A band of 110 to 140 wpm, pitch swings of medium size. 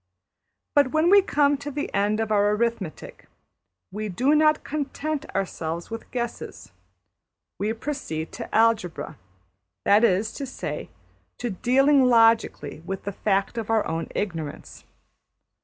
No: slow, 135 wpm; wide, 5.9 semitones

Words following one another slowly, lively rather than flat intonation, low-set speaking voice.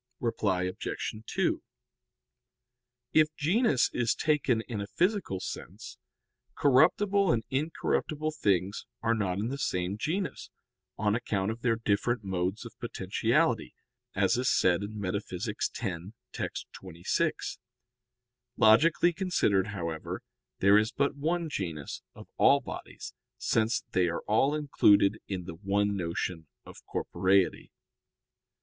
Yes: slow, 125 wpm; wide, 6.9 semitones; low, 110 Hz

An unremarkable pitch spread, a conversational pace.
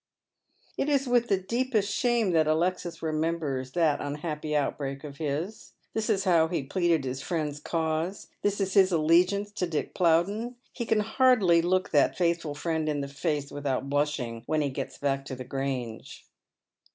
Yes: average, 5.0 semitones; average, 175 wpm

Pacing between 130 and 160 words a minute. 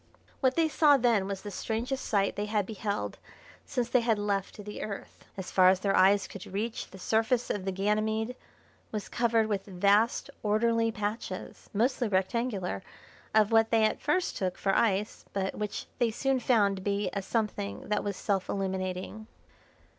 No: average, 175 wpm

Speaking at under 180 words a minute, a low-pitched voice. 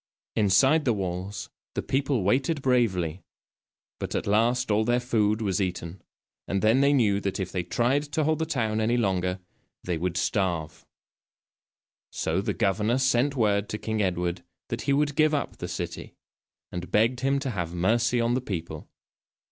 Yes: average, 170 wpm; low, 110 Hz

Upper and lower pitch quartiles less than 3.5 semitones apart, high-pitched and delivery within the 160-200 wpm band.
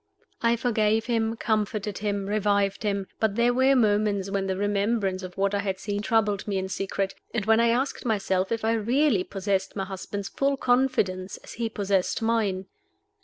Yes: narrow, 2.6 semitones; high, 205 Hz; average, 180 wpm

